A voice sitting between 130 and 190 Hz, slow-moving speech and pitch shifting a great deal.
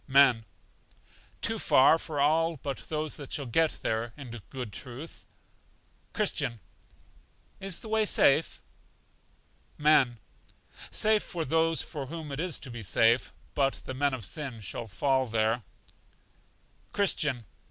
No: medium, 140 Hz; slow, 130 wpm; average, 4.9 semitones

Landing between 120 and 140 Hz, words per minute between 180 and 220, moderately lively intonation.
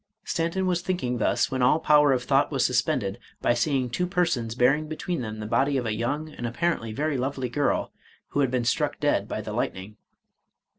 Yes: low, 135 Hz; average, 200 wpm; average, 4.6 semitones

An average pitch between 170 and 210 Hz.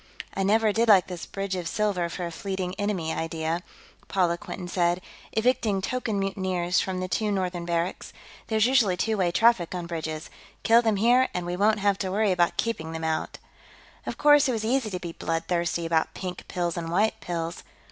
Yes: medium, 185 Hz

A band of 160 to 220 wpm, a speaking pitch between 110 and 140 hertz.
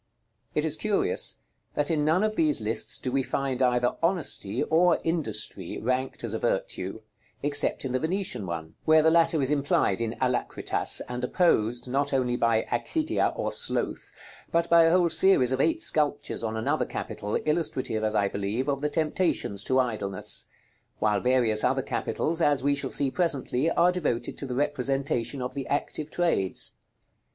Yes: average, 170 wpm; low, 135 Hz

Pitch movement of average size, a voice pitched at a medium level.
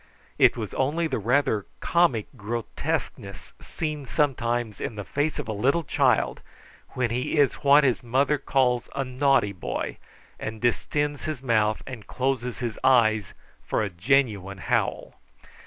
No: average, 4.2 semitones; low, 125 Hz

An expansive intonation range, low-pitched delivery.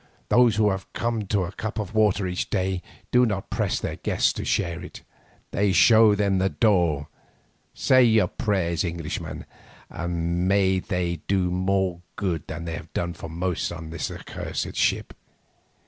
No: average, 3.1 semitones; very low, 95 Hz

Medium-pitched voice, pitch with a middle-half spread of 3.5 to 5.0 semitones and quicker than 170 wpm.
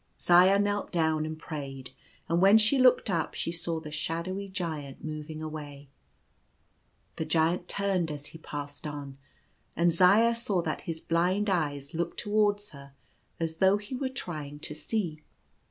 No: medium, 165 Hz; average, 4.4 semitones; average, 160 wpm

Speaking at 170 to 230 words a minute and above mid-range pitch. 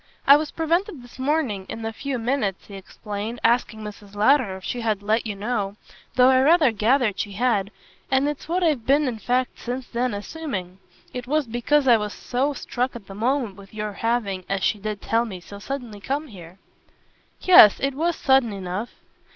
Yes: average, 195 wpm; high, 235 Hz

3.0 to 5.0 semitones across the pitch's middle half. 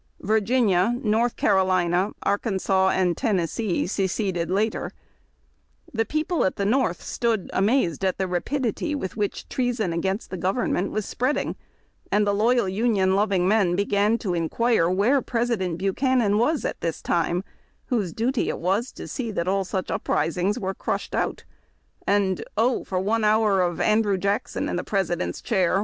Yes: average, 3.6 semitones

